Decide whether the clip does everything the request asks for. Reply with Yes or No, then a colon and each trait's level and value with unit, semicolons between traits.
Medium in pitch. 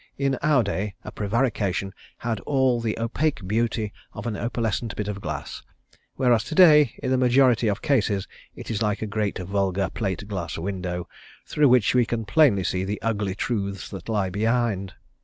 No: low, 110 Hz